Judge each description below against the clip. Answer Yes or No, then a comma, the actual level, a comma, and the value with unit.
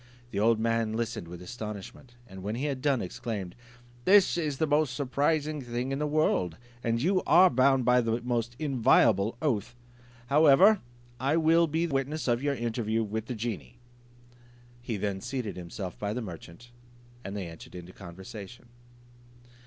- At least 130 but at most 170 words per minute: Yes, average, 160 wpm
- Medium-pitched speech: No, low, 120 Hz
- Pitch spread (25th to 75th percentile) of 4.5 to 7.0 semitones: Yes, average, 5.2 semitones